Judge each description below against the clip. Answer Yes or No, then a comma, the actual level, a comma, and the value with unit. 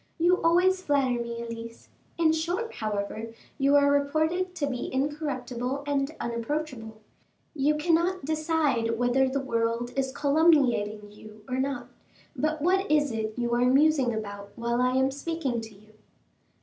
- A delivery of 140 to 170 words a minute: Yes, average, 150 wpm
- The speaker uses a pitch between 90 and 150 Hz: No, very high, 270 Hz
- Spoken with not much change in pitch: No, average, 4.9 semitones